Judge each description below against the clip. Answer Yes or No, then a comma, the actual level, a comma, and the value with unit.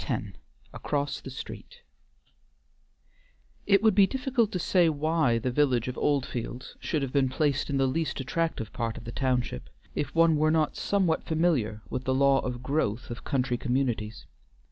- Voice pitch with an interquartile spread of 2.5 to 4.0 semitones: No, average, 4.5 semitones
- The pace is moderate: Yes, average, 165 wpm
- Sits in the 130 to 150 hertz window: Yes, medium, 140 Hz